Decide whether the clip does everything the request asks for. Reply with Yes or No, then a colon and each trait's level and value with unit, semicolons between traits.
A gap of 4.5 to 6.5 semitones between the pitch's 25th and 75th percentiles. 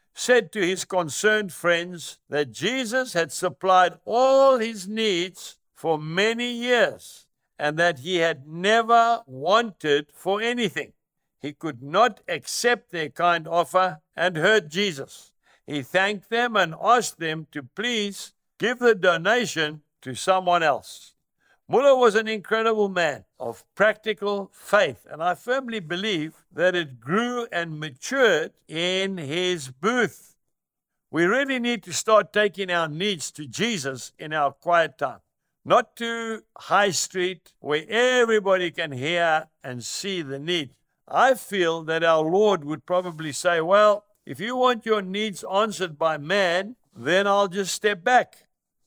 Yes: average, 5.3 semitones